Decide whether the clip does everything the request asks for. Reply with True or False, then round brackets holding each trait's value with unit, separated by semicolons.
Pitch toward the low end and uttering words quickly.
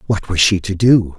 True (95 Hz; 255 wpm)